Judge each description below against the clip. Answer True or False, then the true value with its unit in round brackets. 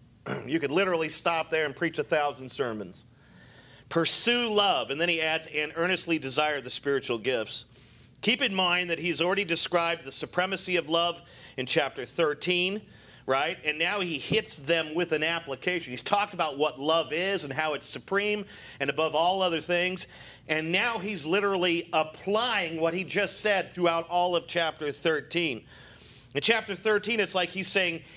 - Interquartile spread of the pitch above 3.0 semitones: True (3.7 semitones)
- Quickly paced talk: False (175 wpm)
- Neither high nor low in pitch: True (165 Hz)